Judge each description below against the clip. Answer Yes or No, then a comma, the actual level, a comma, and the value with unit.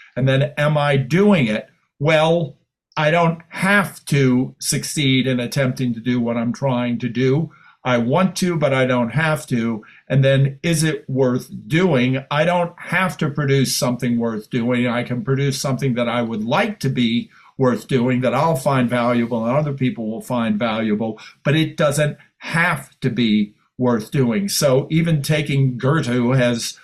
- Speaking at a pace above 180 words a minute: No, average, 175 wpm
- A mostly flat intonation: No, average, 3.9 semitones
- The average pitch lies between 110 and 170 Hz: Yes, low, 135 Hz